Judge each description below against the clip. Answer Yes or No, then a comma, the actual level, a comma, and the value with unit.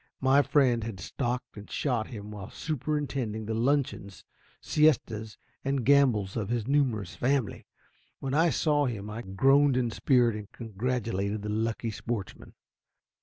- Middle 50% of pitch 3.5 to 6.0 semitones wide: Yes, average, 4.4 semitones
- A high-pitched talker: No, low, 120 Hz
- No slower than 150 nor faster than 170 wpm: No, average, 140 wpm